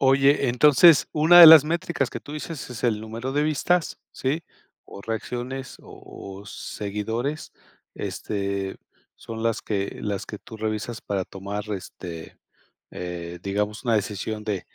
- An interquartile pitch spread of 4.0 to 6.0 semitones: Yes, wide, 5.4 semitones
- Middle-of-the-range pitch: No, low, 110 Hz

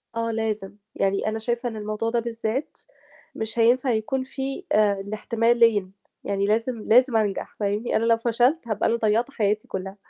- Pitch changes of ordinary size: No, narrow, 2.0 semitones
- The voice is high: Yes, high, 225 Hz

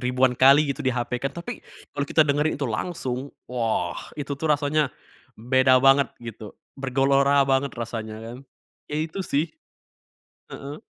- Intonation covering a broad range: No, narrow, 2.5 semitones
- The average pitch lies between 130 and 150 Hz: Yes, low, 135 Hz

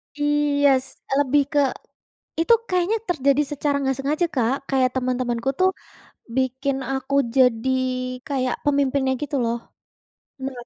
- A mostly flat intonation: Yes, narrow, 2.1 semitones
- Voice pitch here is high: Yes, very high, 270 Hz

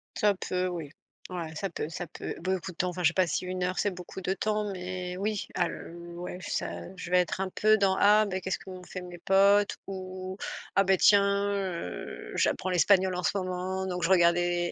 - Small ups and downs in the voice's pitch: Yes, narrow, 1.4 semitones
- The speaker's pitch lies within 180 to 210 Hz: Yes, medium, 185 Hz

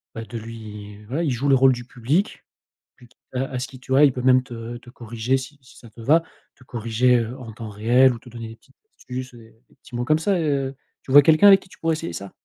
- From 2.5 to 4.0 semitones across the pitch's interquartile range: Yes, average, 2.9 semitones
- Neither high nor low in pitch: No, low, 125 Hz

